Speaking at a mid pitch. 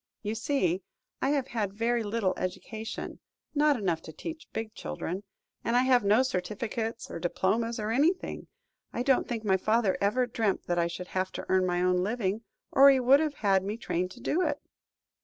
No: high, 220 Hz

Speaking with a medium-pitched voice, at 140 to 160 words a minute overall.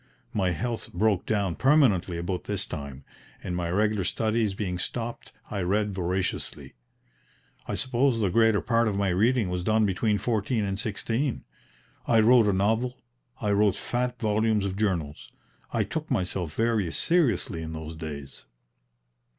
No: low, 105 Hz; average, 150 wpm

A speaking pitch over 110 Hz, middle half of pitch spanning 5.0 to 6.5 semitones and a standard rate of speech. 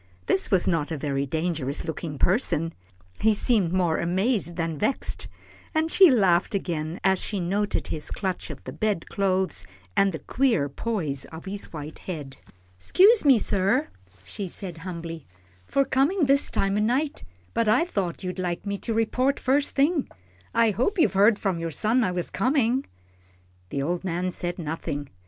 Yes: high, 190 Hz; wide, 5.6 semitones; average, 170 wpm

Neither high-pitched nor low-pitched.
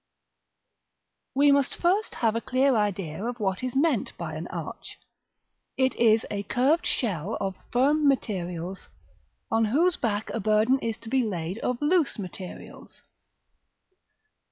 No: high, 230 Hz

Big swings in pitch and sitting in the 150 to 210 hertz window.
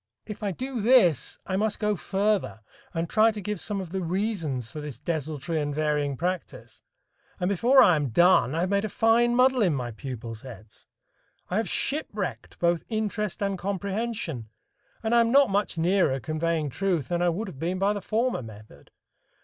Yes: wide, 5.9 semitones; medium, 185 Hz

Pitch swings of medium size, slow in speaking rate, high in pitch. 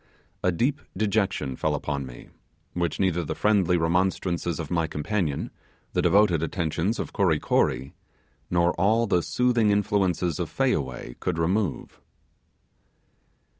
No: average, 3.9 semitones; slow, 130 wpm; very low, 90 Hz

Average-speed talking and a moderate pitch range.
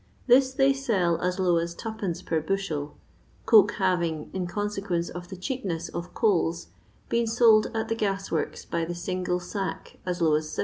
Yes: average, 180 wpm; average, 3.9 semitones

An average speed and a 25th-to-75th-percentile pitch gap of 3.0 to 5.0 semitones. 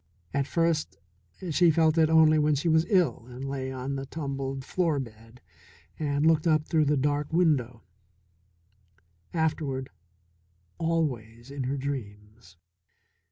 No: slow, 130 wpm; average, 3.4 semitones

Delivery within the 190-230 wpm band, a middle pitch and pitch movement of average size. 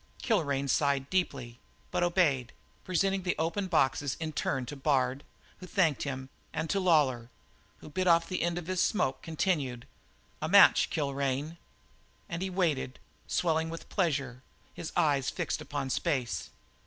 No: average, 150 wpm; medium, 155 Hz; average, 4.6 semitones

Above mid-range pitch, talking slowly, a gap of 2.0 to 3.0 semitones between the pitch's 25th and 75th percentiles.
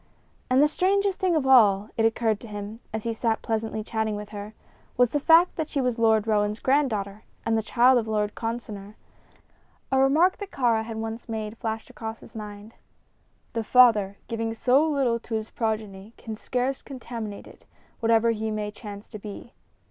No: high, 225 Hz; average, 185 wpm; average, 2.7 semitones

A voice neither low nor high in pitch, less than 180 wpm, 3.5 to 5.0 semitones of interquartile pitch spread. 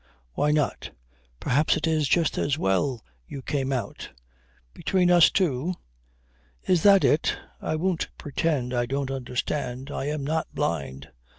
Yes: medium, 145 Hz; average, 140 wpm; average, 4.2 semitones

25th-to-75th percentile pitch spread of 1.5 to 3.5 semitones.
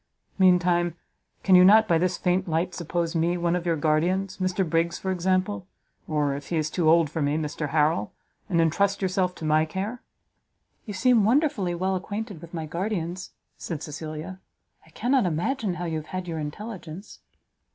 Yes: average, 2.9 semitones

